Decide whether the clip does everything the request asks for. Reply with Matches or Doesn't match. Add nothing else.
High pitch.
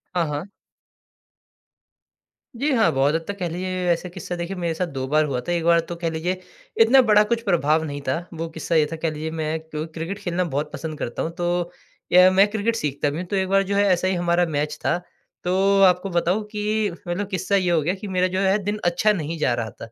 Doesn't match